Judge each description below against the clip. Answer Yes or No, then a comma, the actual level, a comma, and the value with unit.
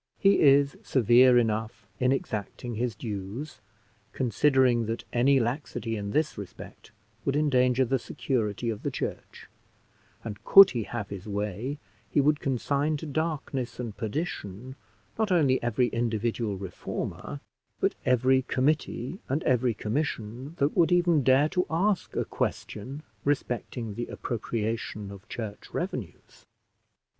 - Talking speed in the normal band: No, slow, 130 wpm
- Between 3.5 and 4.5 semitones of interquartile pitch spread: Yes, average, 4.2 semitones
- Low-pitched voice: Yes, low, 125 Hz